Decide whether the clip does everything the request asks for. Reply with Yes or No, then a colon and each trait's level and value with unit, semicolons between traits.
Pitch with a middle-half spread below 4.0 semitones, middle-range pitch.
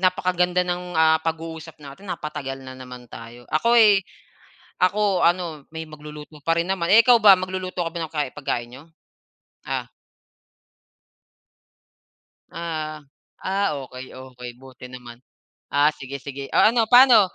No: average, 5.2 semitones; medium, 160 Hz